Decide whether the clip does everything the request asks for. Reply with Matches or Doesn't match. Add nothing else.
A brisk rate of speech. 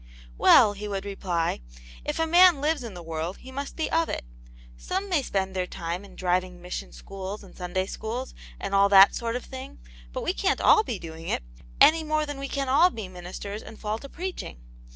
Matches